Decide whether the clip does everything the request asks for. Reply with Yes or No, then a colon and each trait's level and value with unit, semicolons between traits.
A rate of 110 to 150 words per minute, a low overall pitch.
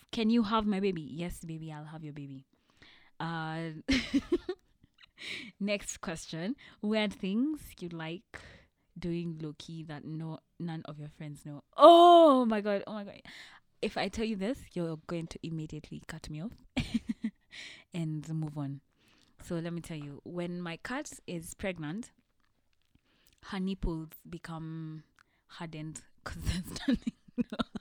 No: average, 140 wpm; medium, 170 Hz